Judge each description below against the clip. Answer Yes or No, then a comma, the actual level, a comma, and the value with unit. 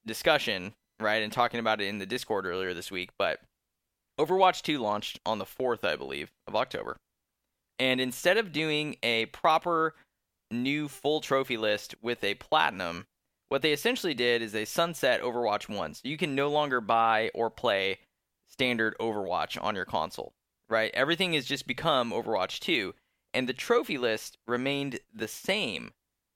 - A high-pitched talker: No, low, 125 Hz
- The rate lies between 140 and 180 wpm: Yes, average, 165 wpm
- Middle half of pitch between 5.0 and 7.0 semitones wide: Yes, average, 5.3 semitones